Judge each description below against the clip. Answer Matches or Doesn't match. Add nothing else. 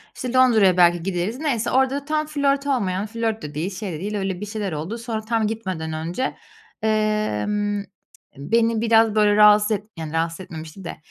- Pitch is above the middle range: Matches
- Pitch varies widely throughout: Doesn't match